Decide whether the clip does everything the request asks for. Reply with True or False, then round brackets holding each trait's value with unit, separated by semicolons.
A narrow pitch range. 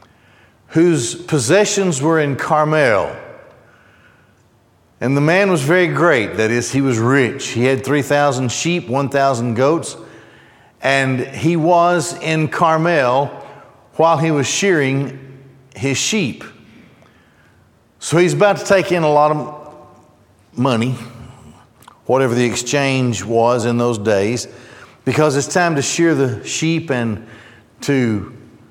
False (5.1 semitones)